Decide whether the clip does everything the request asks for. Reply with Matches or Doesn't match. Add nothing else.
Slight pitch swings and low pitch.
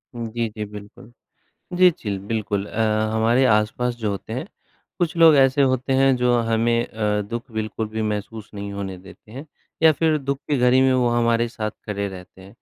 Doesn't match